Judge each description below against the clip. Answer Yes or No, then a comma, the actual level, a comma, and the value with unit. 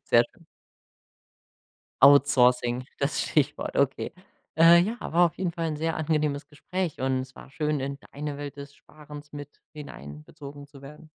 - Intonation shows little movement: Yes, narrow, 1.8 semitones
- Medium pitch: Yes, medium, 145 Hz